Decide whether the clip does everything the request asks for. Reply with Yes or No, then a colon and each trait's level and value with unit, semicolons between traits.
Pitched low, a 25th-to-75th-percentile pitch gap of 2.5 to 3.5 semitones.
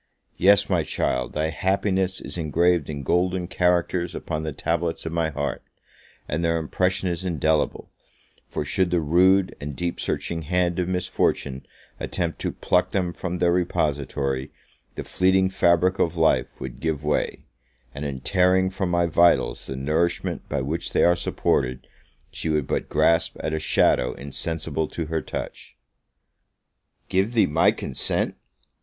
Yes: very low, 85 Hz; average, 2.9 semitones